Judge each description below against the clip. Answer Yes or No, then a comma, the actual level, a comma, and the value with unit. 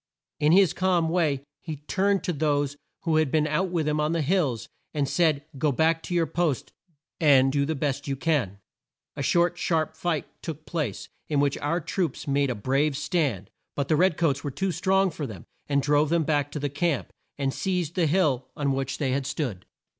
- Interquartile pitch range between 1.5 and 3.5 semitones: Yes, average, 3.2 semitones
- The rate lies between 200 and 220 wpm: Yes, fast, 205 wpm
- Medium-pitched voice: Yes, medium, 150 Hz